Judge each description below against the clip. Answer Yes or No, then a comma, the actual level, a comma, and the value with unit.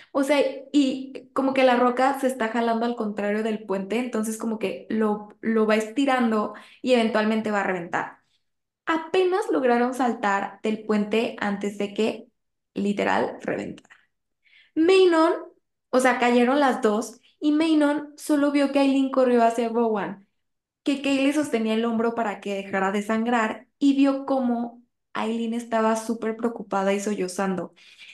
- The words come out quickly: No, average, 150 wpm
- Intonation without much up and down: No, average, 4.0 semitones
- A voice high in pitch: Yes, high, 235 Hz